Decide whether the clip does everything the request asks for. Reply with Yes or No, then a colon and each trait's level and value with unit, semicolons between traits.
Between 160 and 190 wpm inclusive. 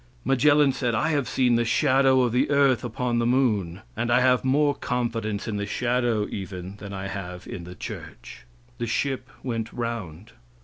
Yes: average, 180 wpm